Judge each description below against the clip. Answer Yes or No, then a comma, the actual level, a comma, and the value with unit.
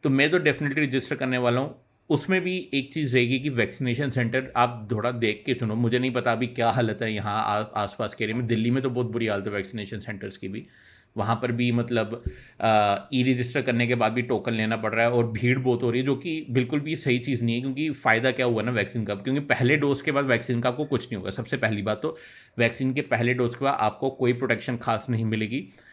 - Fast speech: Yes, fast, 250 wpm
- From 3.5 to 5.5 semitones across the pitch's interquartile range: No, average, 2.7 semitones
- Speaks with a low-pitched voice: Yes, low, 125 Hz